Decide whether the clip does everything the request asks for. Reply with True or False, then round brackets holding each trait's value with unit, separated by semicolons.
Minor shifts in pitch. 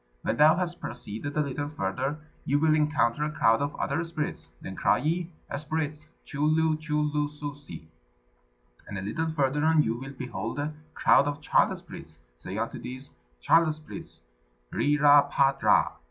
True (2.3 semitones)